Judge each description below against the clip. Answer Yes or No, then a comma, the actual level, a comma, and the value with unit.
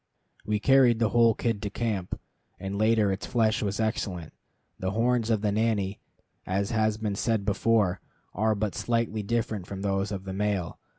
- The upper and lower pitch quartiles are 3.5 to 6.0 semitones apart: No, narrow, 2.4 semitones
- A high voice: No, low, 105 Hz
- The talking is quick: No, average, 175 wpm